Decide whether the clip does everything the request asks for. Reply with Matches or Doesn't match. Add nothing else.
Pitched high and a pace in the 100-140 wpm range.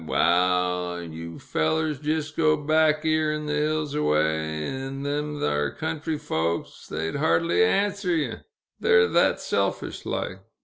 Doesn't match